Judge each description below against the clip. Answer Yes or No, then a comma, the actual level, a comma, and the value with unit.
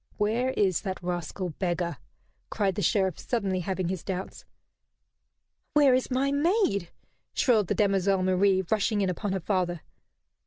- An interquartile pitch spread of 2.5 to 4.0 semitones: Yes, average, 2.9 semitones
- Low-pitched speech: No, high, 195 Hz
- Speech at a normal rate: Yes, average, 145 wpm